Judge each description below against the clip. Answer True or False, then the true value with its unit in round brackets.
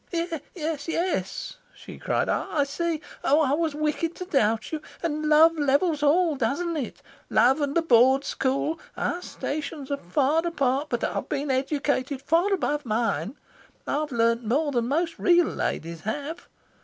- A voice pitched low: False (290 Hz)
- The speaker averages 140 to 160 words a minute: True (155 wpm)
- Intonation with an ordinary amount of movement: True (3.6 semitones)